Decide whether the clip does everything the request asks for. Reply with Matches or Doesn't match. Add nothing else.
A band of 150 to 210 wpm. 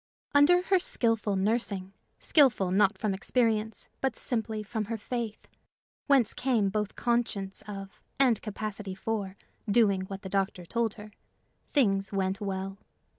Doesn't match